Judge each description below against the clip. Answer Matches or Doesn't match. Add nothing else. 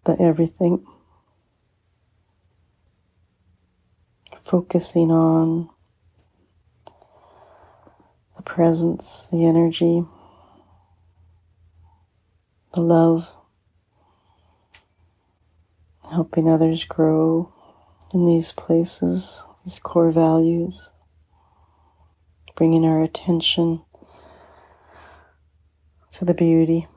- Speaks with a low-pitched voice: Matches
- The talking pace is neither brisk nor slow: Doesn't match